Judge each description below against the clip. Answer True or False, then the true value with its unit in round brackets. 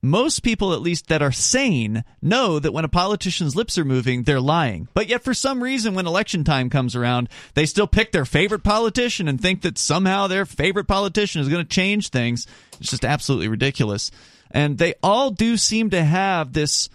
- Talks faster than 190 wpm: True (200 wpm)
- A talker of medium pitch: True (165 Hz)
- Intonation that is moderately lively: False (6.7 semitones)